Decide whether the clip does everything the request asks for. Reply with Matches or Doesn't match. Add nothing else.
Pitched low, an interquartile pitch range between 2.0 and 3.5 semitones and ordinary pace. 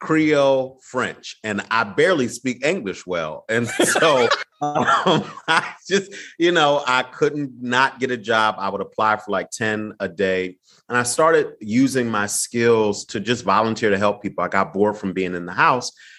Doesn't match